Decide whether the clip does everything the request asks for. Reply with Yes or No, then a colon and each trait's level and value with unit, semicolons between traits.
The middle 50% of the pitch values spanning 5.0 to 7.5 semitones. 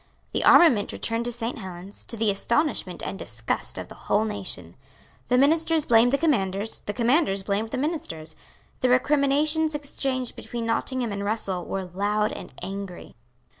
Yes: wide, 5.6 semitones